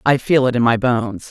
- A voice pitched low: Yes, low, 125 Hz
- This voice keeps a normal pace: No, fast, 275 wpm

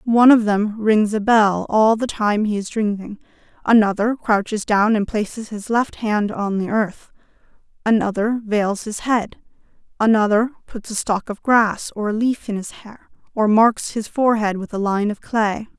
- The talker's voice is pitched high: Yes, high, 215 Hz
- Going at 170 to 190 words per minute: Yes, average, 180 wpm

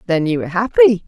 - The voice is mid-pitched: No, high, 205 Hz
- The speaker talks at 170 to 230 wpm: Yes, fast, 225 wpm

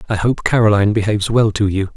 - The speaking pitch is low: Yes, low, 105 Hz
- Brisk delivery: Yes, fast, 215 wpm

